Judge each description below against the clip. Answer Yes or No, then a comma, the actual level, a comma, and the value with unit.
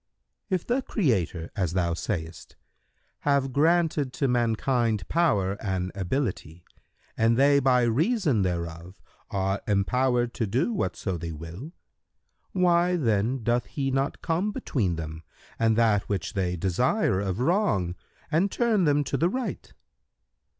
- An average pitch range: No, wide, 7.6 semitones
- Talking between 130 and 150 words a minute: Yes, slow, 135 wpm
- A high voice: No, low, 115 Hz